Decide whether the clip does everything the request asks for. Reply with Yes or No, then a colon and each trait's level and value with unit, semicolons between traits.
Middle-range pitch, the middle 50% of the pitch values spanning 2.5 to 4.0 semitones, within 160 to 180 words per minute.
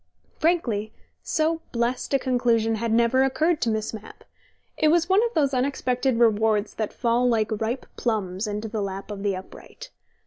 No: high, 235 Hz; average, 3.7 semitones; average, 170 wpm